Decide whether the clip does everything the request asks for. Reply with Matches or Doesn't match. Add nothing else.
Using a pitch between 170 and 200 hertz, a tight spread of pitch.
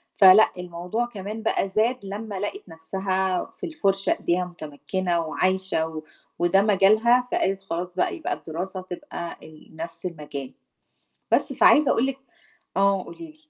Doesn't match